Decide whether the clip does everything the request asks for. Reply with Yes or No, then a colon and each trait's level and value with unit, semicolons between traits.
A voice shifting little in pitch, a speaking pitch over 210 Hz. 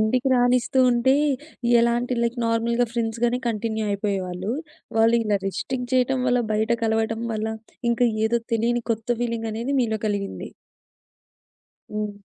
Yes: narrow, 2.0 semitones; high, 230 Hz